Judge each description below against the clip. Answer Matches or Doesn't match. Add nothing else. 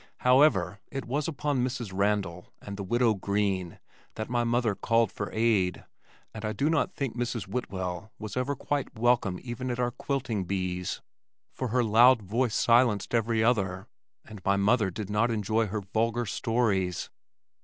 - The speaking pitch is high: Doesn't match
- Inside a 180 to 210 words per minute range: Doesn't match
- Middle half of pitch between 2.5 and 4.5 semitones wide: Matches